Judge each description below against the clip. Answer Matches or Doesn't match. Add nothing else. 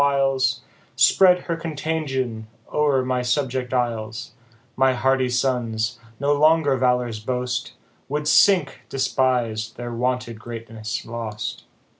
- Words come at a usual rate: Doesn't match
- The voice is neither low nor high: Doesn't match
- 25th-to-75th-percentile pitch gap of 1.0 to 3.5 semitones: Matches